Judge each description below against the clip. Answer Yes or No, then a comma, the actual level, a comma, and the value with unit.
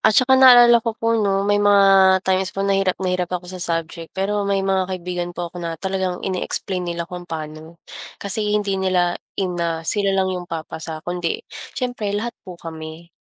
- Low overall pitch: No, medium, 185 Hz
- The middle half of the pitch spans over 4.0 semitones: No, narrow, 2.5 semitones